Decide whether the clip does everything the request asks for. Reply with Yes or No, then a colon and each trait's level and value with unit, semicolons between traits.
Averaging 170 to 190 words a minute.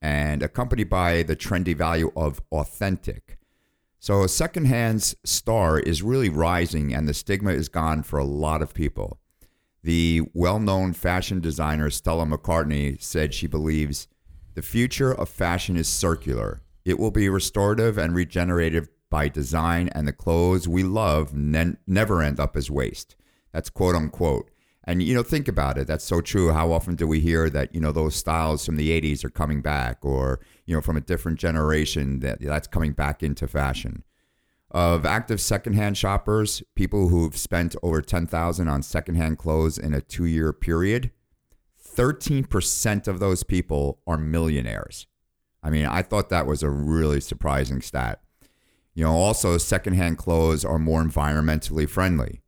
No: average, 160 wpm